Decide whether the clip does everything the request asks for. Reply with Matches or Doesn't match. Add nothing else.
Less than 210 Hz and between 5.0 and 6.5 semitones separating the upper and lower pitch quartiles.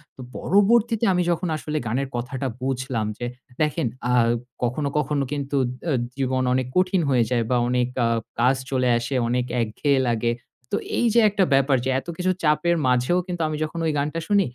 Matches